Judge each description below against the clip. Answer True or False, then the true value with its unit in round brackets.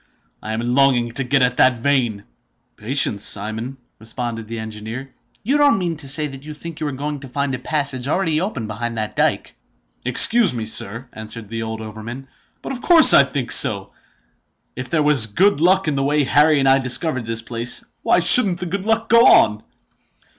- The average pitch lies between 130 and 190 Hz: True (135 Hz)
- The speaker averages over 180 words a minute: True (200 wpm)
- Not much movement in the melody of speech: False (4.9 semitones)